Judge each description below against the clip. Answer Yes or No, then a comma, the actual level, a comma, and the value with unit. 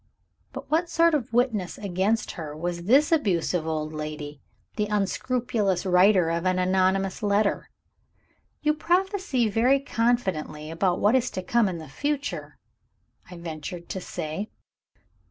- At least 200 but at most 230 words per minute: No, slow, 135 wpm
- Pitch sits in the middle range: No, high, 195 Hz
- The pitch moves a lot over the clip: Yes, wide, 6.3 semitones